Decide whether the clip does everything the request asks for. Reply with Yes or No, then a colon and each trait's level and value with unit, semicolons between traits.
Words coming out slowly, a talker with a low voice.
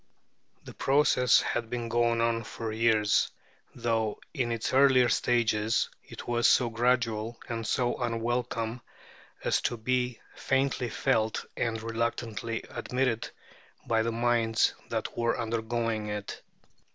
Yes: slow, 125 wpm; low, 115 Hz